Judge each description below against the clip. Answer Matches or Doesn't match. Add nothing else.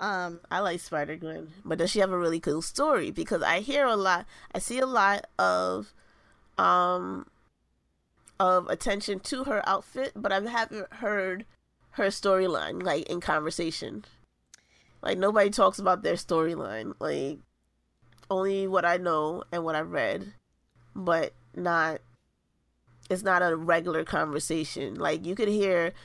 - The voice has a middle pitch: Matches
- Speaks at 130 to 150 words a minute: Matches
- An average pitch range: Matches